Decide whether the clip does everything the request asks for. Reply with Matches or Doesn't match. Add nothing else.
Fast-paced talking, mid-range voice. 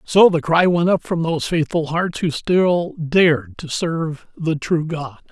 Doesn't match